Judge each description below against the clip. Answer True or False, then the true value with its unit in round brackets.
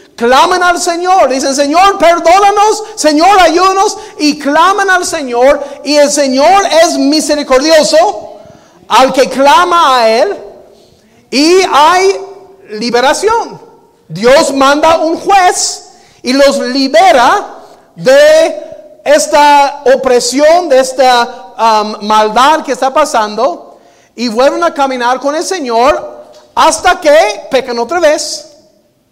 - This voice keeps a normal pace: False (110 wpm)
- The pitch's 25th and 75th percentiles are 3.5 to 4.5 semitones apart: False (5.0 semitones)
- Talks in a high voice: True (305 Hz)